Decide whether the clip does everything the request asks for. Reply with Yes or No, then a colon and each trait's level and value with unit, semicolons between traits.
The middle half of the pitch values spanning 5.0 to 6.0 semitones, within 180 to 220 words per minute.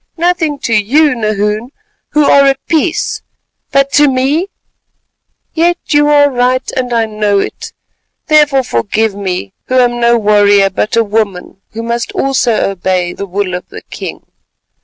No: wide, 5.4 semitones; average, 150 wpm